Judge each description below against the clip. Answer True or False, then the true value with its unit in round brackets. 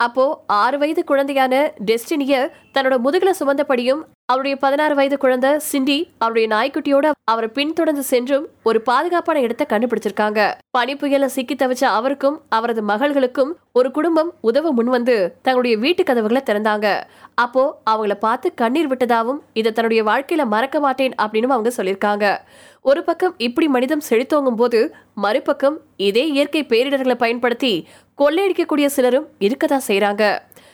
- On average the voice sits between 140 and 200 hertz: False (265 Hz)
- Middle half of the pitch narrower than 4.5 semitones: True (4.1 semitones)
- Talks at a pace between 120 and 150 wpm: True (130 wpm)